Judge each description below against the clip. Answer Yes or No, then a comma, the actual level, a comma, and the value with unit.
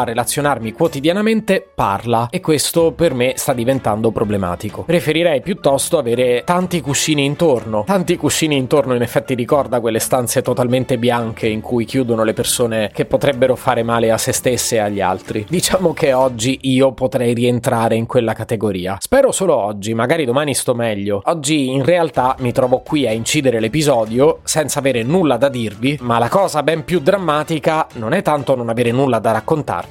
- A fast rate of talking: Yes, fast, 175 wpm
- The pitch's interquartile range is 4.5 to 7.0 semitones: Yes, average, 5.0 semitones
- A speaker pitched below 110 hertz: No, low, 130 Hz